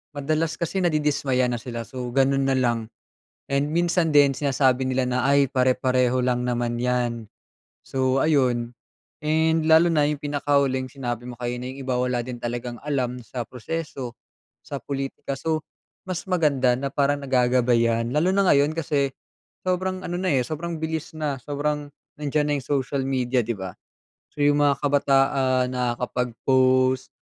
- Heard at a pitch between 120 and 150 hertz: Yes, low, 135 Hz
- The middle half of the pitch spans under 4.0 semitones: Yes, average, 2.9 semitones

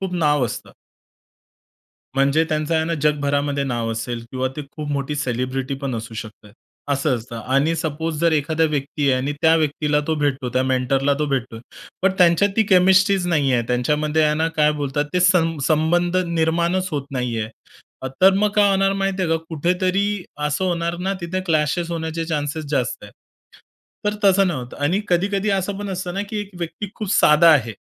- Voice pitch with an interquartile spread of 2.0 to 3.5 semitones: No, average, 4.3 semitones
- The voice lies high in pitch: No, medium, 155 Hz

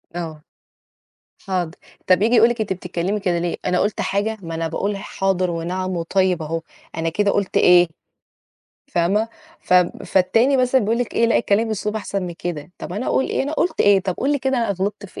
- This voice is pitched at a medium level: No, high, 195 Hz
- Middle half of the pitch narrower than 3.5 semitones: No, average, 3.8 semitones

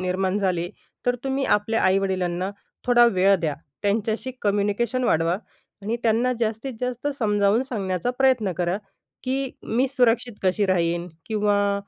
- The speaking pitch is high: Yes, high, 205 Hz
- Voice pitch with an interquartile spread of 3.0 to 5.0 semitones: Yes, average, 4.4 semitones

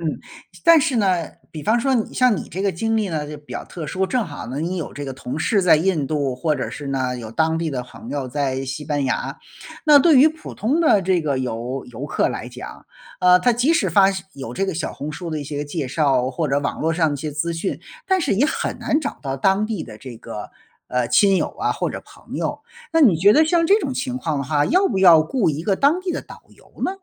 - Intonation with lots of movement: Yes, wide, 7.7 semitones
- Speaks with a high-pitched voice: No, medium, 165 Hz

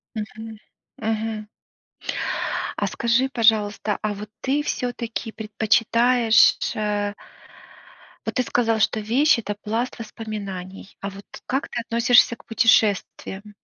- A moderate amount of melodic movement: No, narrow, 2.0 semitones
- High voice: Yes, high, 220 Hz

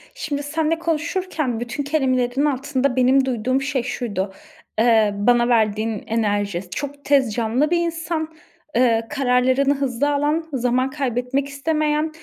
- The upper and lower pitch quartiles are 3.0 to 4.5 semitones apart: Yes, average, 3.5 semitones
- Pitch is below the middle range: No, very high, 265 Hz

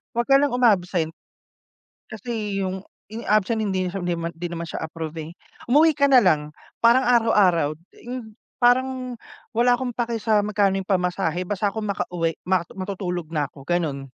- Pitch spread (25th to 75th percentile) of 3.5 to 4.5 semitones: No, average, 5.2 semitones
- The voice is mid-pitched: No, high, 200 Hz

